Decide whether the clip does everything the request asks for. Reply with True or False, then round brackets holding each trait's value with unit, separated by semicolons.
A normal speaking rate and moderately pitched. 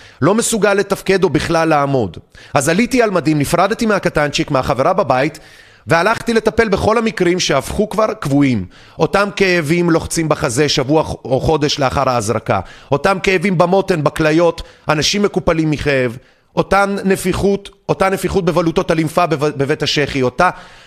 True (130 wpm; 165 Hz)